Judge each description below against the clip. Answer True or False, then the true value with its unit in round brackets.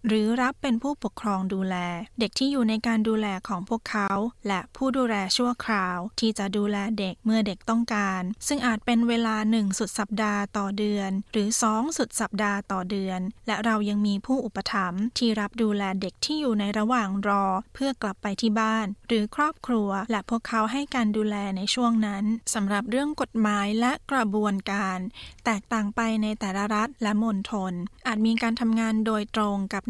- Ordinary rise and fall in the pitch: False (2.3 semitones)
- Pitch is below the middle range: False (215 Hz)